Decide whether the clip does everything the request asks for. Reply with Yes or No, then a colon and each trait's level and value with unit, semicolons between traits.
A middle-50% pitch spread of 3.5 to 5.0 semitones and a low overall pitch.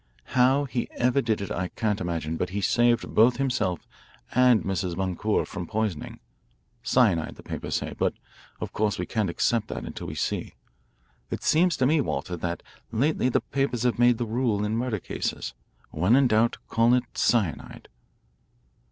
Yes: average, 4.5 semitones; low, 115 Hz